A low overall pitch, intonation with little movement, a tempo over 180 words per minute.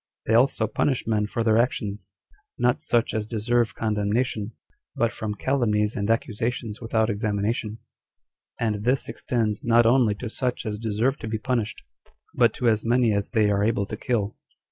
No: low, 110 Hz; narrow, 2.2 semitones; average, 165 wpm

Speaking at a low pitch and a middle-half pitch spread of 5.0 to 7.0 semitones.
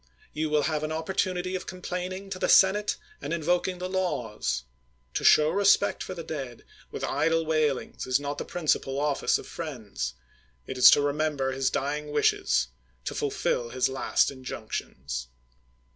No: medium, 150 Hz; wide, 5.5 semitones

